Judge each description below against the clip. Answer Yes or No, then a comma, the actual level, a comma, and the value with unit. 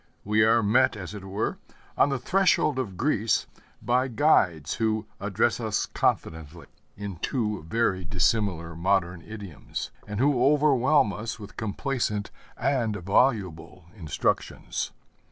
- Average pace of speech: No, slow, 125 wpm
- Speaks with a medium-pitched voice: No, low, 105 Hz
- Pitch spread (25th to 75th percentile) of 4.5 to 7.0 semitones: Yes, average, 5.1 semitones